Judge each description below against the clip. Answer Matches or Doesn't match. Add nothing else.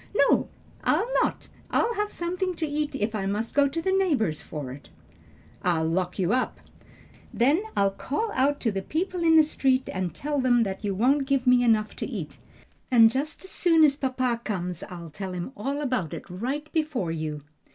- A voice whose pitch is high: Matches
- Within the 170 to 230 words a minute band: Matches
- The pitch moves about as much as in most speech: Doesn't match